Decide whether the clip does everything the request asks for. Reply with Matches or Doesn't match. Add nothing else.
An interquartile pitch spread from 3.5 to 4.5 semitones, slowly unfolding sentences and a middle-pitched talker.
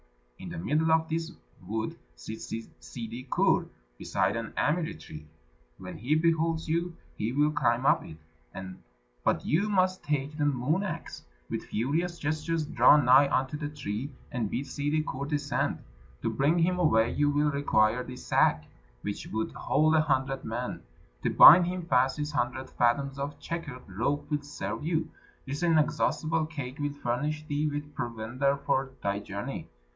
Doesn't match